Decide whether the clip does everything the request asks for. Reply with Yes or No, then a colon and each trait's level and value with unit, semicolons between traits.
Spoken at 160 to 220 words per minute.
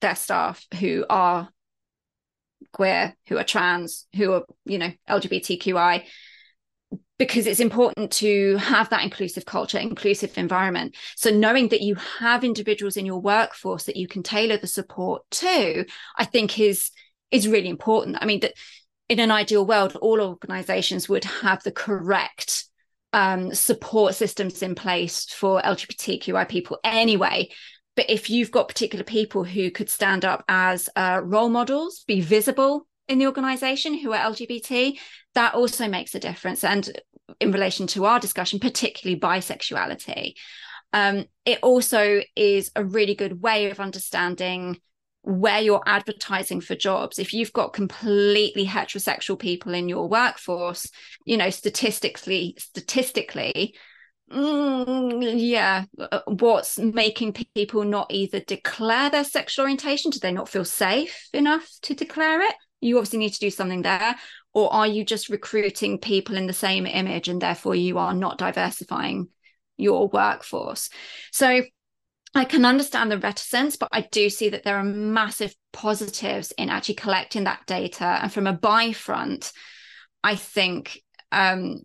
No: average, 145 wpm